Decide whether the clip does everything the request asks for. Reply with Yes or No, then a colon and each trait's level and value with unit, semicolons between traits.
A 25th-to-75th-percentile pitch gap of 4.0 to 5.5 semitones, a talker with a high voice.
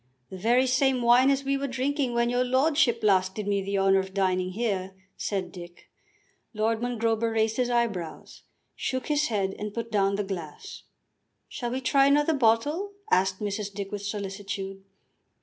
Yes: average, 4.5 semitones; high, 220 Hz